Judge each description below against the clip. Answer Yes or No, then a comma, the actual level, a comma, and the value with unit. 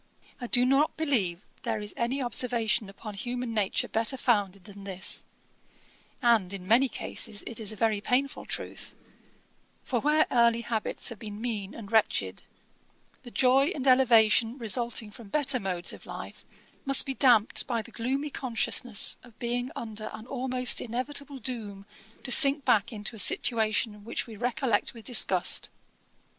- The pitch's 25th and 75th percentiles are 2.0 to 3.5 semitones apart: Yes, average, 3.1 semitones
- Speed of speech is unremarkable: Yes, average, 155 wpm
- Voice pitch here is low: No, high, 235 Hz